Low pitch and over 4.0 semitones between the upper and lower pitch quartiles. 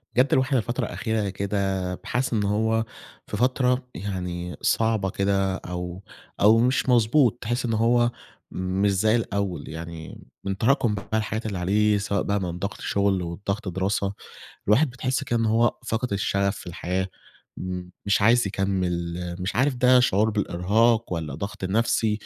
No: low, 105 Hz; average, 3.5 semitones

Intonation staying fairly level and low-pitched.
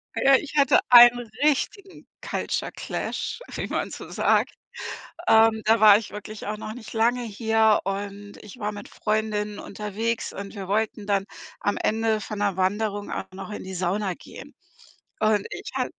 No: narrow, 1.7 semitones; high, 215 Hz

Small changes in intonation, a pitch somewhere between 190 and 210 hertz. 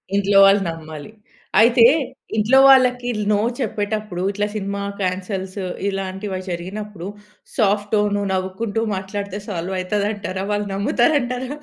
Yes: narrow, 2.2 semitones; high, 205 Hz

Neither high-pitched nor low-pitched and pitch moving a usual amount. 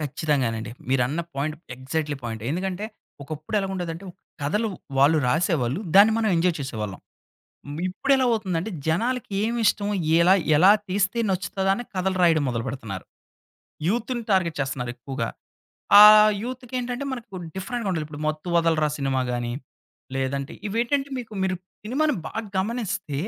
No: medium, 175 Hz; wide, 7.6 semitones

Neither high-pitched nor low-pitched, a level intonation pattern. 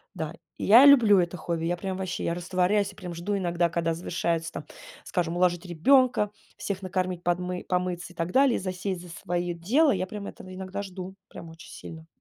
Yes: medium, 180 Hz; narrow, 2.2 semitones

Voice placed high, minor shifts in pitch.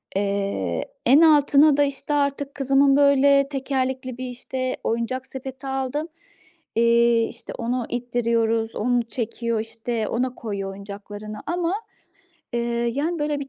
No: very high, 255 Hz; average, 3.4 semitones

